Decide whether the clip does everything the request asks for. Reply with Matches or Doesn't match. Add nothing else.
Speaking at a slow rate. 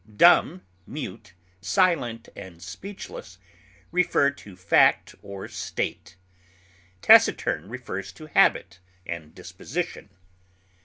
Matches